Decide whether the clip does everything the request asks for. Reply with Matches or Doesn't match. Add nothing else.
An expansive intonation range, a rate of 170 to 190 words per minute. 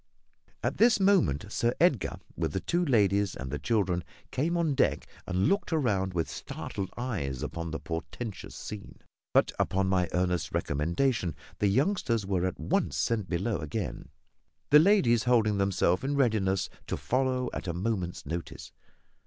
Doesn't match